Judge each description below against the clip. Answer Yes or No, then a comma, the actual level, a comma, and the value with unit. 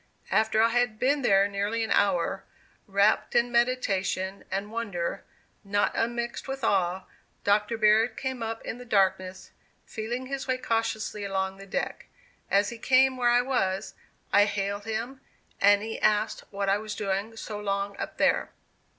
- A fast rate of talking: No, average, 160 wpm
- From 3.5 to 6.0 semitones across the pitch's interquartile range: No, average, 3.1 semitones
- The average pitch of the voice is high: Yes, high, 215 Hz